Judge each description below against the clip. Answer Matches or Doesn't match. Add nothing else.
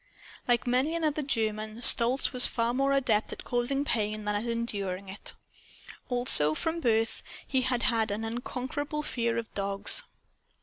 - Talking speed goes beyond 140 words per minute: Matches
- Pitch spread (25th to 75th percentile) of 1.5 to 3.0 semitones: Doesn't match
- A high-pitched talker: Matches